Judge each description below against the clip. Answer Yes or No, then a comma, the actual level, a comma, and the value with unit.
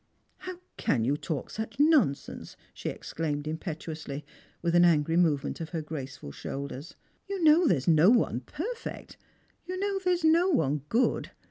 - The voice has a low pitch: No, medium, 170 Hz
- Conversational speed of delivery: Yes, average, 170 wpm